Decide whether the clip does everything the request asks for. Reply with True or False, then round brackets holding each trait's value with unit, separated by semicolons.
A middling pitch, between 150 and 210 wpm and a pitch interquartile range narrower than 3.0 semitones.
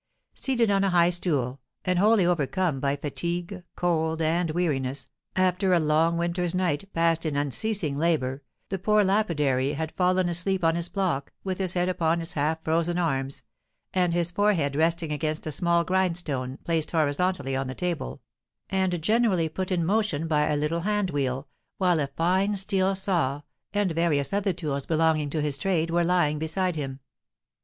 False (170 Hz; 170 wpm; 3.5 semitones)